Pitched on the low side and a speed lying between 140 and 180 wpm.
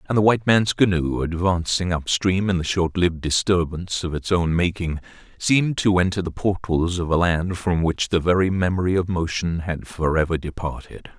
Yes: very low, 90 Hz; average, 175 wpm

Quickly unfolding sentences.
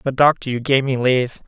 Yes: fast, 245 wpm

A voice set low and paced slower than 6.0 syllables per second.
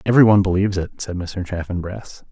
No: very low, 95 Hz; 6.5 syllables/s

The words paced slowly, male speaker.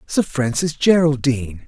Yes: slow, 105 wpm; male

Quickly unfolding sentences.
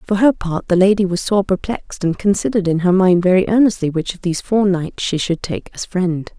Yes: fast, 235 wpm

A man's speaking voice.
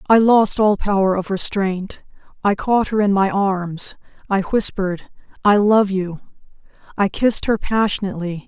No: female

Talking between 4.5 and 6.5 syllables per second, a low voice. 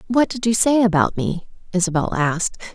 No: 5.5 syllables/s; high, 195 Hz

